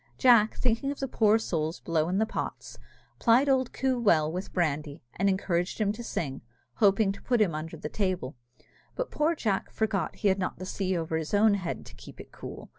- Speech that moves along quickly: Yes, fast, 215 wpm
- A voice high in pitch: Yes, high, 195 Hz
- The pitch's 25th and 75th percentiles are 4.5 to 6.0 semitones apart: Yes, average, 5.1 semitones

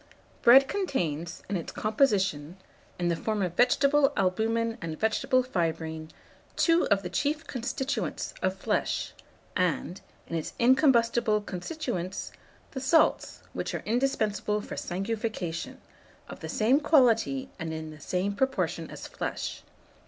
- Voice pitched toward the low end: No, high, 215 Hz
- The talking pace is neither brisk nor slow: No, slow, 130 wpm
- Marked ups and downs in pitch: Yes, wide, 6.8 semitones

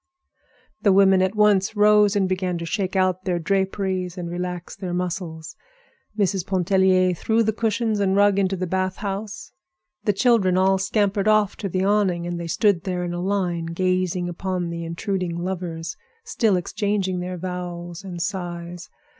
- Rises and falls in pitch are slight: Yes, narrow, 2.1 semitones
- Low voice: No, medium, 185 Hz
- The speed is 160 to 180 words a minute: Yes, average, 165 wpm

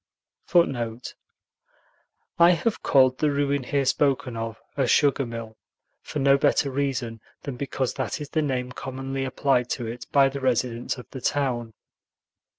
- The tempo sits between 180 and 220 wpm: No, average, 155 wpm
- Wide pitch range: No, narrow, 2.4 semitones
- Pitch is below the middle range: Yes, low, 130 Hz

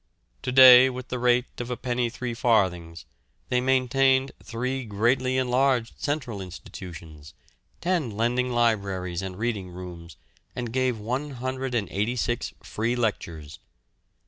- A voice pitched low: Yes, low, 120 Hz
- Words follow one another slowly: Yes, slow, 120 wpm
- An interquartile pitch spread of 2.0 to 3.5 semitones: No, average, 4.3 semitones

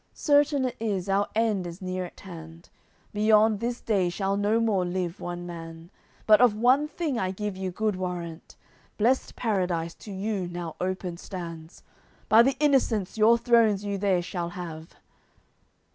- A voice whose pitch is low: No, high, 195 Hz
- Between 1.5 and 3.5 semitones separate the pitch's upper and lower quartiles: No, average, 4.0 semitones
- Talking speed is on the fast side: No, average, 160 wpm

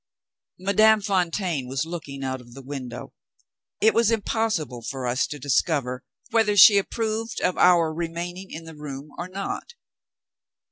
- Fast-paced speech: No, average, 145 wpm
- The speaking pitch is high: No, medium, 170 Hz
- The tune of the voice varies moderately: No, wide, 6.6 semitones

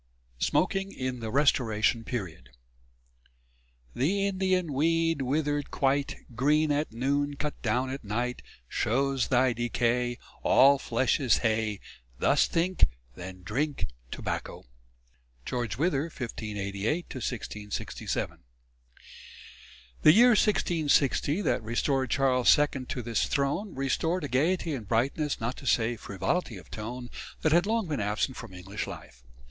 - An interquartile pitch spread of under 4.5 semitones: No, average, 4.8 semitones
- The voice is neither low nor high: No, low, 130 Hz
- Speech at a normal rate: No, slow, 130 wpm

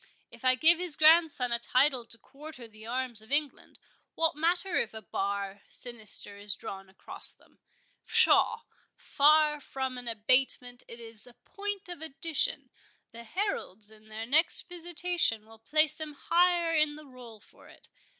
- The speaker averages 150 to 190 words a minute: Yes, average, 155 wpm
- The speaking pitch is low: No, very high, 260 Hz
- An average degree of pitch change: No, wide, 5.8 semitones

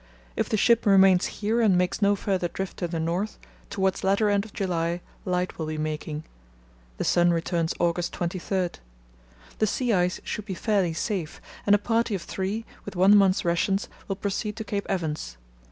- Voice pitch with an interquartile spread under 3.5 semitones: Yes, average, 2.9 semitones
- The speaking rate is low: No, average, 185 wpm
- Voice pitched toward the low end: No, high, 190 Hz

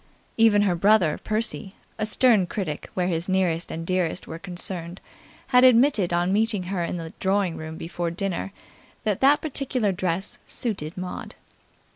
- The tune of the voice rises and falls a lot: No, average, 3.9 semitones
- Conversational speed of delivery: Yes, average, 155 wpm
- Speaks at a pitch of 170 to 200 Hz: Yes, high, 190 Hz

